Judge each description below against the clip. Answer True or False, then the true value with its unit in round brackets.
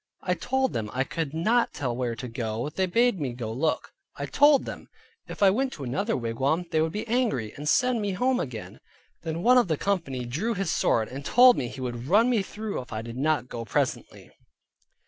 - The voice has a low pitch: False (160 Hz)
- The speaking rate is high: True (220 wpm)